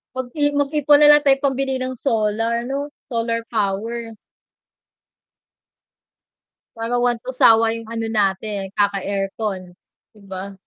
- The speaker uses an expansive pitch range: No, average, 3.9 semitones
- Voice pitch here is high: Yes, high, 230 Hz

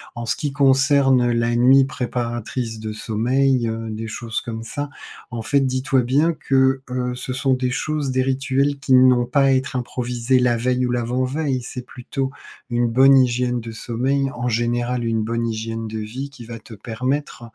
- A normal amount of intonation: No, narrow, 2.3 semitones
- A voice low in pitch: Yes, low, 125 Hz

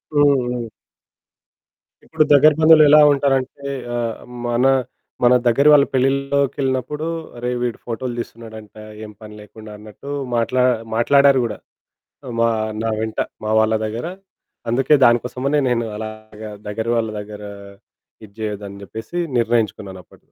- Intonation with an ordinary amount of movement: Yes, average, 4.0 semitones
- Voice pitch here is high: No, low, 120 Hz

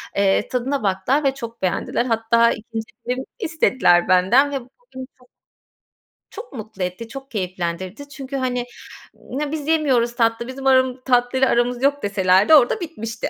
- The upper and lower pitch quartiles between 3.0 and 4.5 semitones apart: Yes, average, 3.7 semitones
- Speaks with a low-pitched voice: No, high, 245 Hz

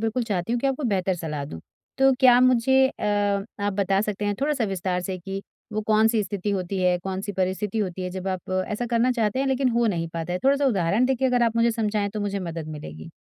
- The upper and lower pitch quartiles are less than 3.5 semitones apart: No, average, 4.6 semitones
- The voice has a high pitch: Yes, high, 205 Hz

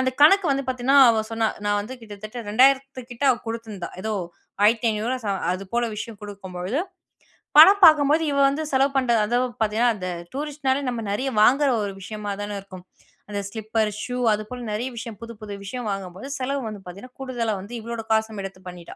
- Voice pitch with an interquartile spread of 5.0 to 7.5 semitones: No, average, 3.9 semitones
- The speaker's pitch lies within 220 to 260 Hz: Yes, high, 230 Hz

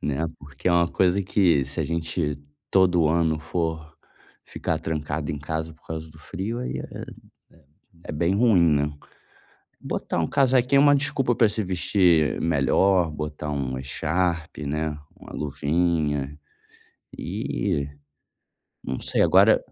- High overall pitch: No, very low, 80 Hz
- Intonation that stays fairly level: No, average, 3.6 semitones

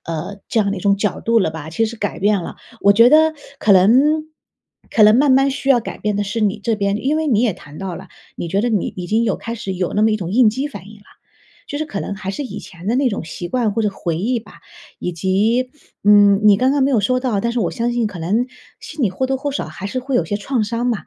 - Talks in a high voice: Yes, high, 210 Hz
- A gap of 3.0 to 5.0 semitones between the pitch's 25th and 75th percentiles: Yes, average, 3.8 semitones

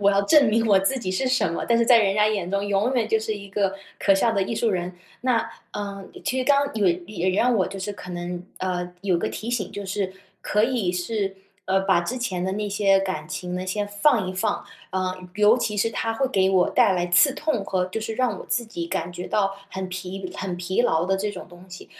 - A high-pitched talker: Yes, high, 200 Hz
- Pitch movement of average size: Yes, average, 3.1 semitones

